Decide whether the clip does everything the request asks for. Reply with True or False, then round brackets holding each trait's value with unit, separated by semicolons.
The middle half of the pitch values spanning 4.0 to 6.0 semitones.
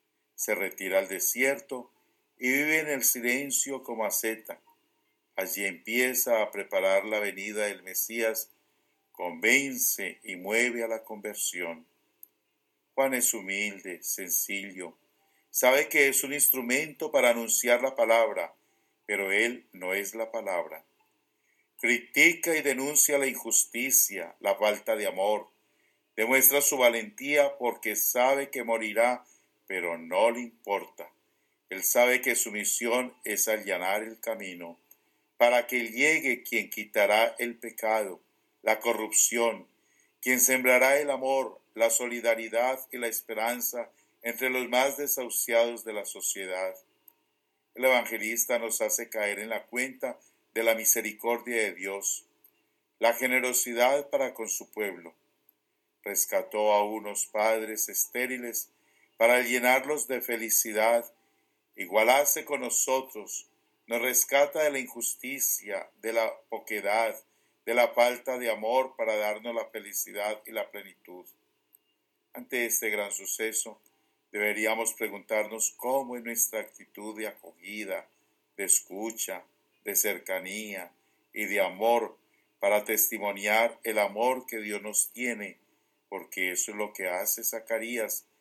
False (3.0 semitones)